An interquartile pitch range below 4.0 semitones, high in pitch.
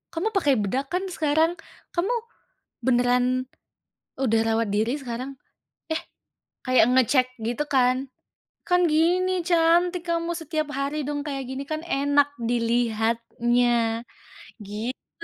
No: average, 5.3 semitones; very high, 270 Hz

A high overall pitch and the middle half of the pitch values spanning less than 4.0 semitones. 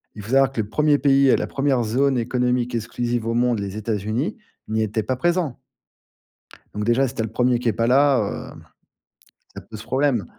No: low, 120 Hz; average, 3.5 semitones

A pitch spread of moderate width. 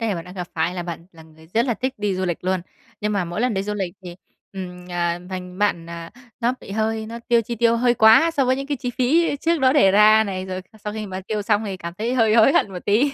Yes: average, 4.5 semitones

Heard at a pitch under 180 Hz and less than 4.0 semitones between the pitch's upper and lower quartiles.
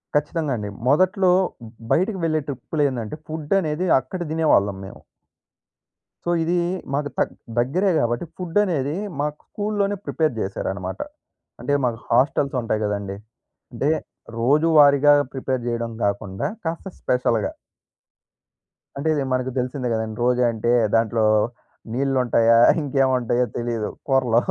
No: low, 135 Hz; average, 5.0 semitones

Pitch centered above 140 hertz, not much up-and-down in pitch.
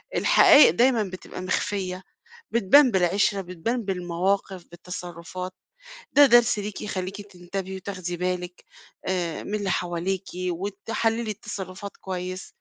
Yes: high, 190 Hz; narrow, 2.3 semitones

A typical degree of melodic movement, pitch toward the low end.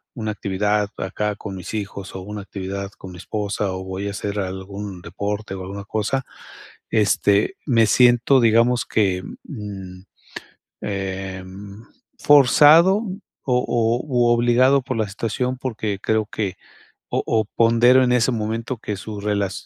Yes: average, 3.3 semitones; low, 105 Hz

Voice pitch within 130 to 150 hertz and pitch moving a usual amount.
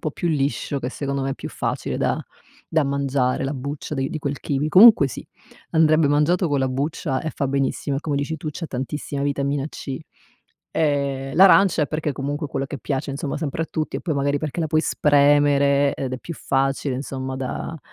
No: medium, 140 Hz; narrow, 2.0 semitones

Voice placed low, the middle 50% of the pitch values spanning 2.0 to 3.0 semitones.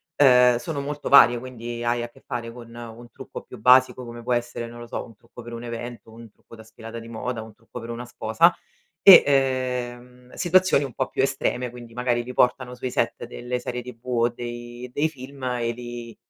No: low, 120 Hz; narrow, 1.3 semitones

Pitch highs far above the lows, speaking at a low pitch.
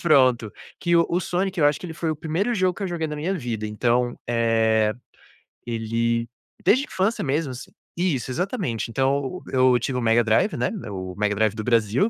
Yes: wide, 7.0 semitones; low, 130 Hz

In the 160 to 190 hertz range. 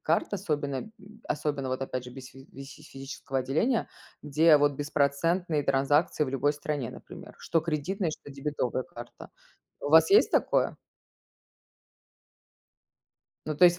No: medium, 145 Hz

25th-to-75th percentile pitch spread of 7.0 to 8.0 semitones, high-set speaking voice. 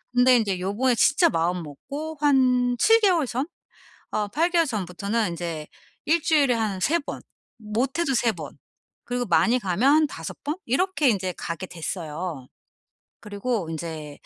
Yes: wide, 7.7 semitones; high, 230 Hz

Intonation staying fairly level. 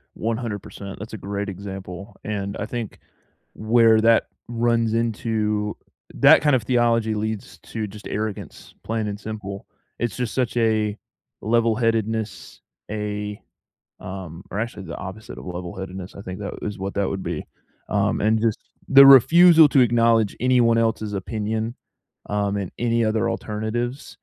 Yes: narrow, 2.3 semitones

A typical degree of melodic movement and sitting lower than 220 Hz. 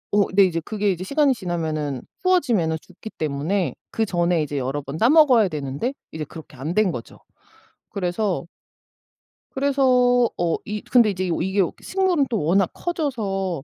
No: wide, 7.3 semitones; high, 190 Hz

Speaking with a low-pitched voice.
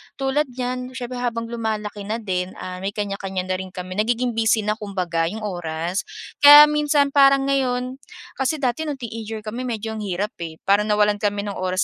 No: high, 220 Hz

